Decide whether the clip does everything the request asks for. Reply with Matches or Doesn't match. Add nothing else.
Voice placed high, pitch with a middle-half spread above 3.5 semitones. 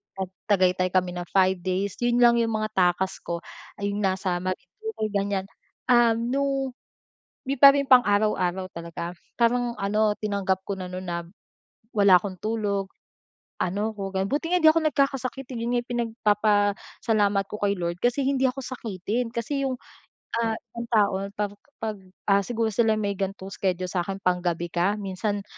Matches